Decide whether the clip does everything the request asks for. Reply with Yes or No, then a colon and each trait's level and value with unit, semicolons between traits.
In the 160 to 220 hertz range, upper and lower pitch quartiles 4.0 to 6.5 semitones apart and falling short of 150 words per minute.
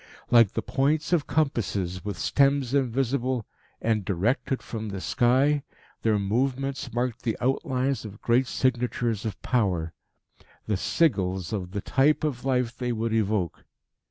No: low, 120 Hz; average, 4.3 semitones; average, 140 wpm